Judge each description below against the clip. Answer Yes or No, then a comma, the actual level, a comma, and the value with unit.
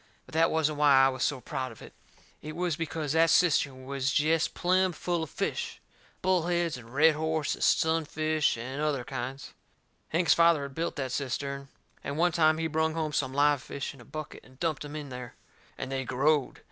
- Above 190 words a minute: Yes, average, 200 wpm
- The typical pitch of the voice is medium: Yes, medium, 150 Hz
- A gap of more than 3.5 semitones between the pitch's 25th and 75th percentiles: No, average, 3.2 semitones